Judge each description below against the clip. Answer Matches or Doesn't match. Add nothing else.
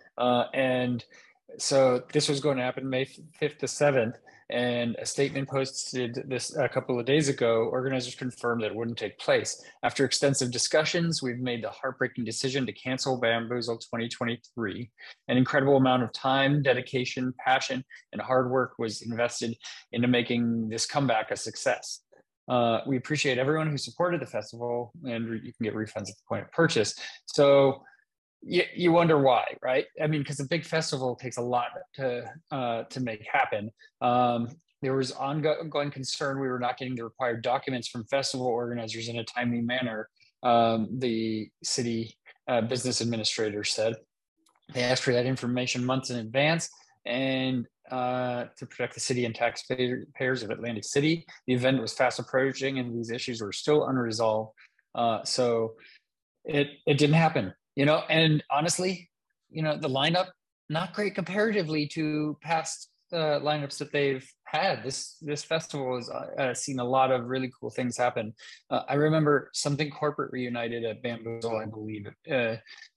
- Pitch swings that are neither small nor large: Matches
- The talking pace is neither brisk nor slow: Matches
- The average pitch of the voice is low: Matches